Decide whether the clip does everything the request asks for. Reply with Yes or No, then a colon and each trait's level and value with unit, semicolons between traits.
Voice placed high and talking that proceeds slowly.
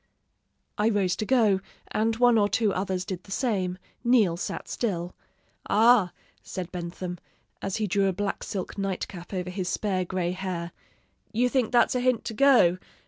No: high, 195 Hz; average, 175 wpm